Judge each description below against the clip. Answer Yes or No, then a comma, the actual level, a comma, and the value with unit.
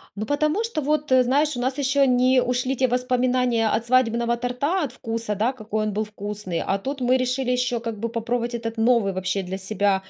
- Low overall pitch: No, high, 245 Hz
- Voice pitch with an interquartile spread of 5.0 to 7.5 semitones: No, average, 3.0 semitones